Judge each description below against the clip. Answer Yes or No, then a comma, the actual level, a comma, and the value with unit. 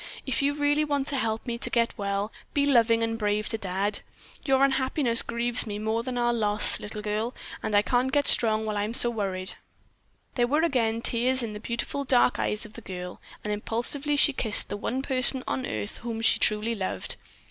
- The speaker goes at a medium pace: No, fast, 210 wpm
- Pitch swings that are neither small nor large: Yes, average, 3.6 semitones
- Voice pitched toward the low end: No, high, 230 Hz